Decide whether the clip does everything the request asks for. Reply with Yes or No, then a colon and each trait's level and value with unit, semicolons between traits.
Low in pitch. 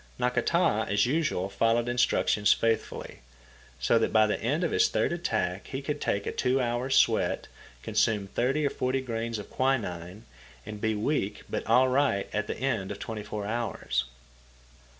Yes: low, 115 Hz